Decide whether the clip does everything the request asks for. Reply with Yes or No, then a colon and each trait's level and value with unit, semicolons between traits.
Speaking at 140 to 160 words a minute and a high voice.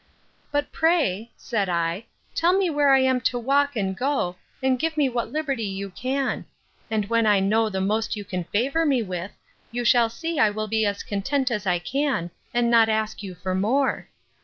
No: average, 200 wpm; high, 230 Hz